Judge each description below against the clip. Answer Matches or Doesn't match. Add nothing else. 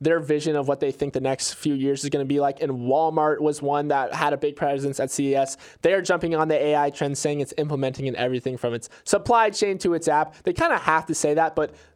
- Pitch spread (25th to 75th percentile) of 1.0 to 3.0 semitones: Matches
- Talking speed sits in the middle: Doesn't match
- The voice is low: Doesn't match